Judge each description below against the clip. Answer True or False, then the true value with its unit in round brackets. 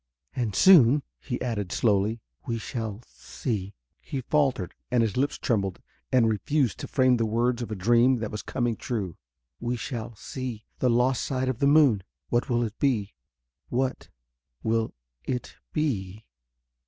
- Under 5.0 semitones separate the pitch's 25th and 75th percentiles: True (2.9 semitones)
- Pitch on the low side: True (120 Hz)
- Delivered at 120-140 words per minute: False (155 wpm)